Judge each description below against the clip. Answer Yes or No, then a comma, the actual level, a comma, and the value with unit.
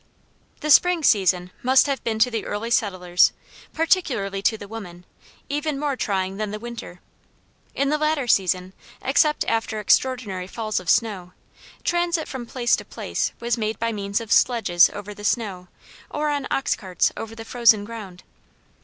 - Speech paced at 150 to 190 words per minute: Yes, average, 165 wpm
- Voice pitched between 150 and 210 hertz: No, high, 225 Hz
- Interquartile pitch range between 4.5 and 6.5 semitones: Yes, average, 5.0 semitones